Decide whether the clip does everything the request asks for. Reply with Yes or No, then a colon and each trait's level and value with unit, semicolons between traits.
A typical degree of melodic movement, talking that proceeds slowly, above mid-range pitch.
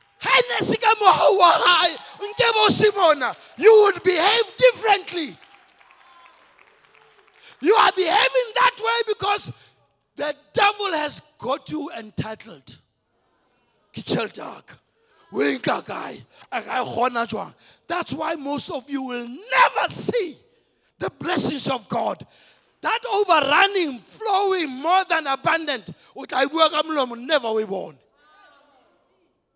No: wide, 7.3 semitones; slow, 75 wpm; very high, 340 Hz